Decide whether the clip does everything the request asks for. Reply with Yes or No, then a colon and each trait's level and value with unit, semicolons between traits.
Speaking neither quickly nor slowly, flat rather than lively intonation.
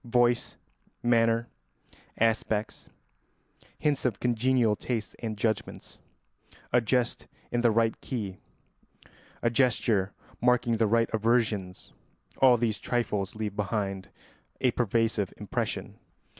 No: slow, 105 wpm; narrow, 2.2 semitones